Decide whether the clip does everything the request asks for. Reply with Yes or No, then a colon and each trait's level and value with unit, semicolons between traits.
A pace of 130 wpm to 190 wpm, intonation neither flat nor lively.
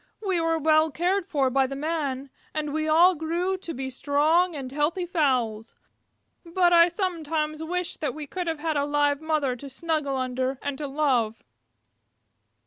Yes: average, 175 wpm; average, 3.4 semitones